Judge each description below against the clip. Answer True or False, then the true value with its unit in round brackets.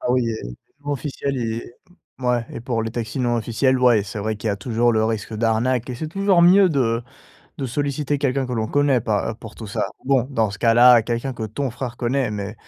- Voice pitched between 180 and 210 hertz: False (120 Hz)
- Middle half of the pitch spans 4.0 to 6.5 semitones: False (3.1 semitones)